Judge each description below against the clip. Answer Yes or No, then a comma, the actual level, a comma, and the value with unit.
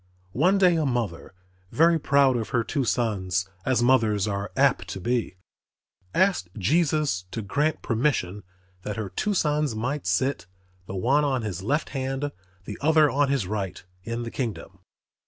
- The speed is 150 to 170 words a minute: Yes, average, 160 wpm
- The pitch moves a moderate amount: No, wide, 6.0 semitones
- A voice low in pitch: Yes, low, 125 Hz